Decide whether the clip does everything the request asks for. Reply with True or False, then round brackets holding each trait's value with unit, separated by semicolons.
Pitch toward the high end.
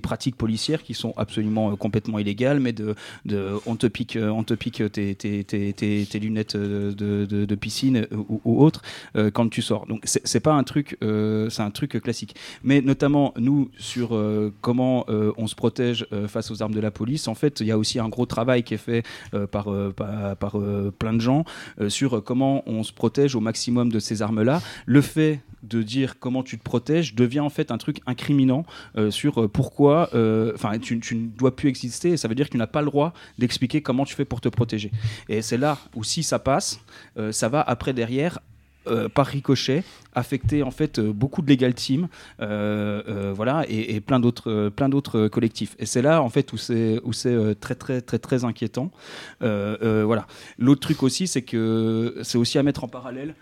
False (115 Hz)